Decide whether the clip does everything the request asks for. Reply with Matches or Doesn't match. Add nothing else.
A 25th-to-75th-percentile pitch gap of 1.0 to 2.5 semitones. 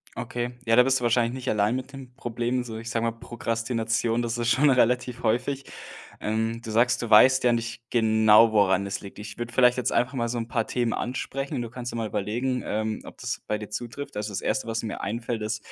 Matches